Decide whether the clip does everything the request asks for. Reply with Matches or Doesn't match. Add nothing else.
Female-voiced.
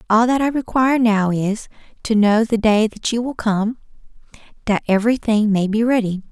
Matches